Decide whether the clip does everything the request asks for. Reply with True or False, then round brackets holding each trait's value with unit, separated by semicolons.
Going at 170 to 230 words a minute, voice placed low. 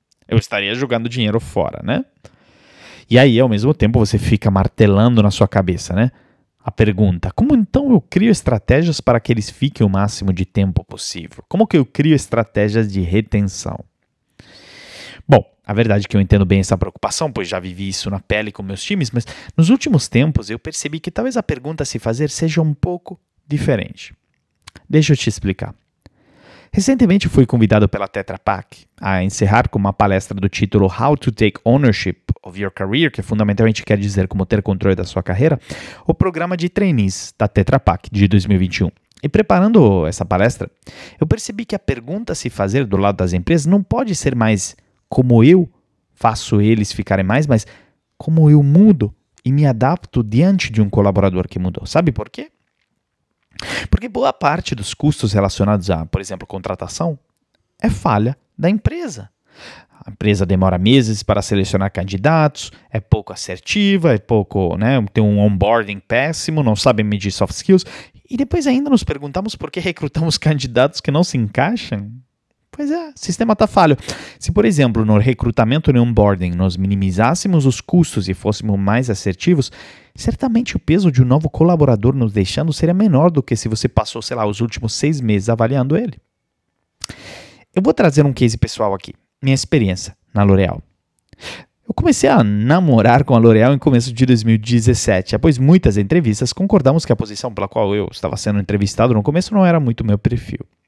True (175 wpm; 115 Hz)